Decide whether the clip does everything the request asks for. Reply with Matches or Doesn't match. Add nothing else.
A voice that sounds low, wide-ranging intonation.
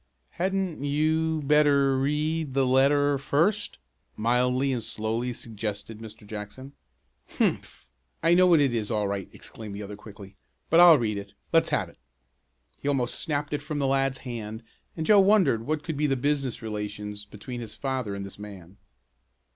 Matches